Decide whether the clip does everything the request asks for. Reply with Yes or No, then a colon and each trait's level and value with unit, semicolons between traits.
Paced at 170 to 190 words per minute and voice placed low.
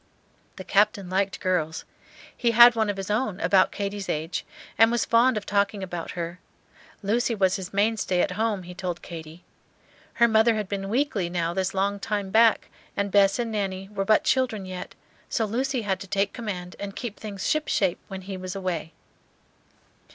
No: average, 185 wpm; high, 200 Hz